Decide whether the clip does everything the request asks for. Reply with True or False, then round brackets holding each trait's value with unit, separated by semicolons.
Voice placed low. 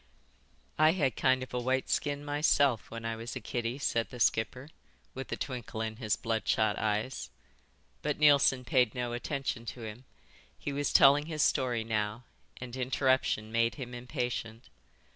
True (125 Hz)